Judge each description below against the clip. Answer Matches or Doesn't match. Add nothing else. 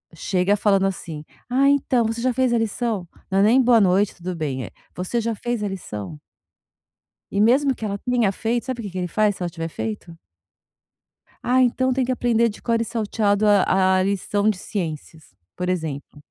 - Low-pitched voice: Doesn't match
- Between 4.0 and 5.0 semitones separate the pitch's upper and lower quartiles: Matches